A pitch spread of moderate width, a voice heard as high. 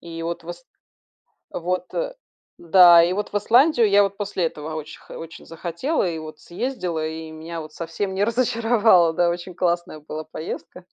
No: average, 3.7 semitones; medium, 175 Hz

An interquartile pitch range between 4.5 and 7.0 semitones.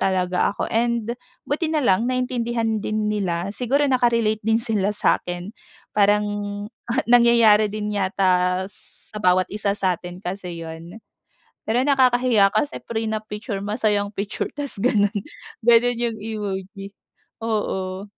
No: average, 3.3 semitones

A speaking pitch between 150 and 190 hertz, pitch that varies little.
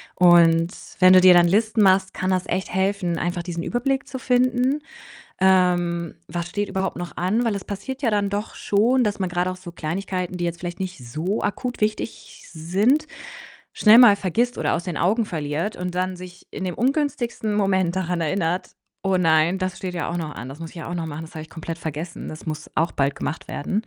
No: medium, 185 Hz; average, 3.2 semitones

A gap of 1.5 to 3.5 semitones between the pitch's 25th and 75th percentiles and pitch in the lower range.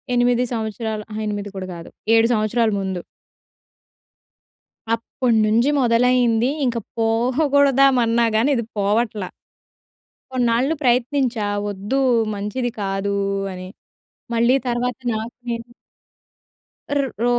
No: narrow, 2.6 semitones; high, 230 Hz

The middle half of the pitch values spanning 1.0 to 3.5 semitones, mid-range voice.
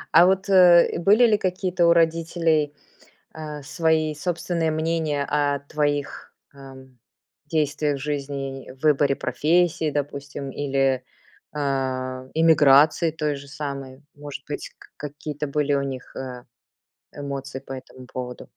Yes: average, 2.8 semitones; medium, 145 Hz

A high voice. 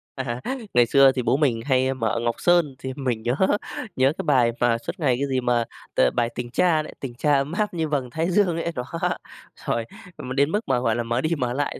No: low, 130 Hz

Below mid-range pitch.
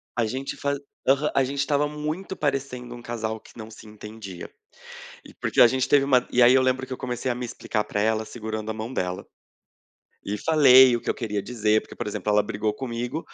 Yes: low, 120 Hz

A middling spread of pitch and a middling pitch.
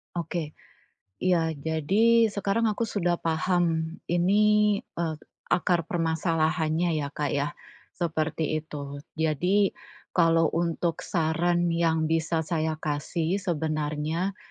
No: narrow, 2.1 semitones; medium, 165 Hz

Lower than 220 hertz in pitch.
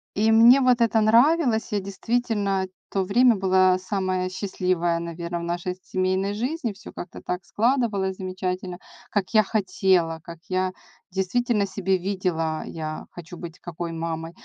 Yes: high, 190 Hz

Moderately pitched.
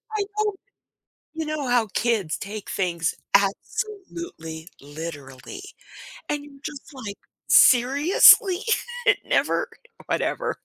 No: high, 245 Hz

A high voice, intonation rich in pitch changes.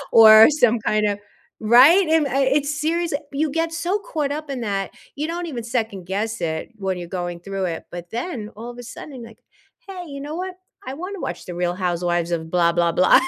Yes: high, 235 Hz; wide, 8.6 semitones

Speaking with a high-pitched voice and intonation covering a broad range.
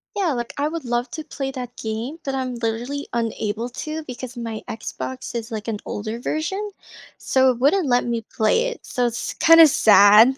No: high, 245 Hz; average, 4.0 semitones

